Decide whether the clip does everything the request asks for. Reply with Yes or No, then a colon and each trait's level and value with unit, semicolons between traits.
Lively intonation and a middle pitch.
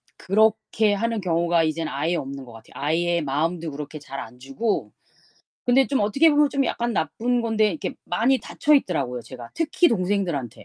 Yes: wide, 7.7 semitones; medium, 175 Hz